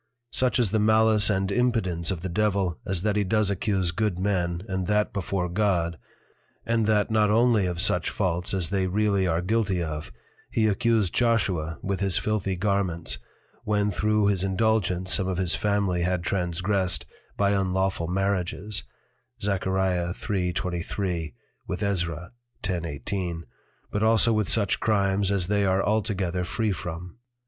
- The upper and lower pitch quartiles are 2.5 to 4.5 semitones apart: Yes, average, 2.8 semitones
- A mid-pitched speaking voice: No, very low, 95 Hz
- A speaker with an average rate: Yes, average, 150 wpm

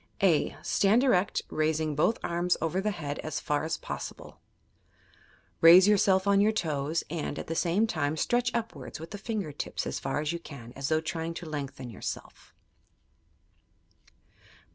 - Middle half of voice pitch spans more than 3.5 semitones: Yes, average, 4.6 semitones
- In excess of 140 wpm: Yes, average, 165 wpm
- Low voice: No, medium, 165 Hz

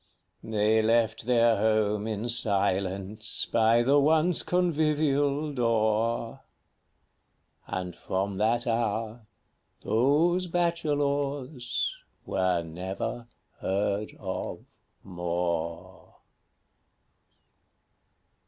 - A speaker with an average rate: No, slow, 70 wpm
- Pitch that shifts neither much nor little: No, wide, 5.7 semitones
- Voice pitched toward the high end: No, low, 115 Hz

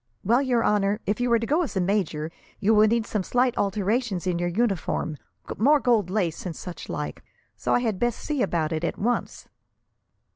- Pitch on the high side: Yes, high, 210 Hz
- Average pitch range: Yes, average, 4.7 semitones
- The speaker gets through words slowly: No, fast, 205 wpm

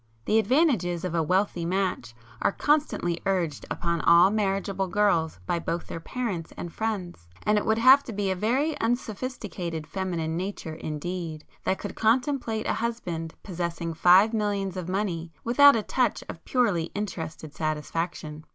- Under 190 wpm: Yes, average, 150 wpm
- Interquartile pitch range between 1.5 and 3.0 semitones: No, average, 4.7 semitones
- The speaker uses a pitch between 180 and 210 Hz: Yes, high, 190 Hz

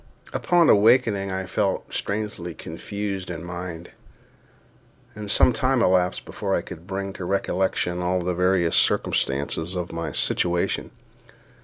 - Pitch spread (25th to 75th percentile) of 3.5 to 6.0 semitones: No, narrow, 2.4 semitones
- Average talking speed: No, slow, 130 wpm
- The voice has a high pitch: No, very low, 95 Hz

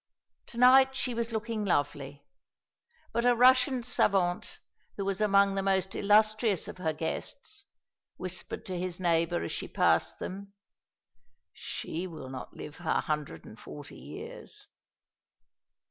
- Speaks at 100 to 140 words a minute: Yes, slow, 135 wpm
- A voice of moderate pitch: No, high, 195 Hz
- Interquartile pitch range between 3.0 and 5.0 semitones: No, wide, 5.6 semitones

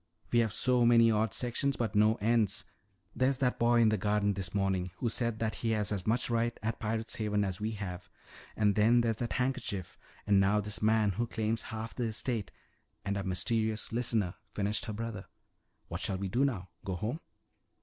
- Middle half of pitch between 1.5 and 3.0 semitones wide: Yes, narrow, 2.4 semitones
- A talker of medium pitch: No, low, 110 Hz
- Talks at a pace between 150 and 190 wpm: No, average, 200 wpm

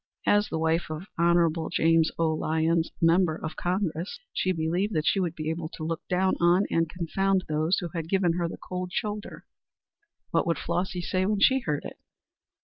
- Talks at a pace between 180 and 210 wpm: Yes, average, 190 wpm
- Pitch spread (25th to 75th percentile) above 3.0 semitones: No, narrow, 2.5 semitones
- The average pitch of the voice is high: No, medium, 170 Hz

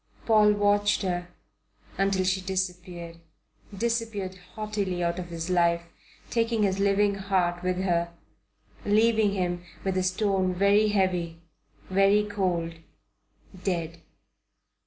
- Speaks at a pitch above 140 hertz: Yes, high, 190 Hz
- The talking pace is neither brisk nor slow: No, slow, 115 wpm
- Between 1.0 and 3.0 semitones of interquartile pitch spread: Yes, narrow, 2.6 semitones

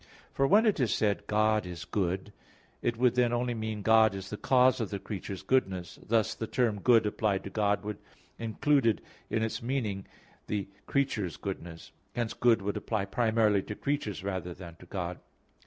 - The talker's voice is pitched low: Yes, low, 110 Hz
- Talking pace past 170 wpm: Yes, average, 180 wpm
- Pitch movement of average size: Yes, average, 3.4 semitones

